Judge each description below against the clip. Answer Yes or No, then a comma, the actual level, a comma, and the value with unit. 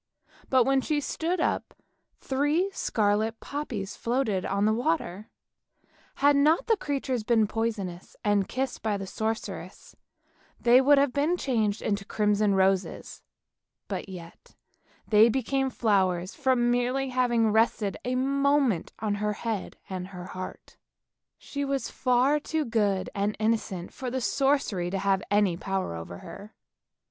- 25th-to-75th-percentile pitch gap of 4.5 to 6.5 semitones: Yes, average, 5.2 semitones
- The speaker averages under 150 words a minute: Yes, average, 140 wpm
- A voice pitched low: No, high, 225 Hz